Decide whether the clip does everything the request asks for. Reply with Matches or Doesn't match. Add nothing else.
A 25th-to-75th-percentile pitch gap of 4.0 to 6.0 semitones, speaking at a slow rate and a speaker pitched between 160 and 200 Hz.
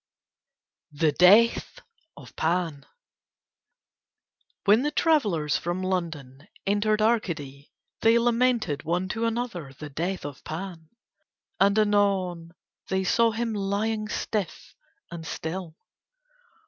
Matches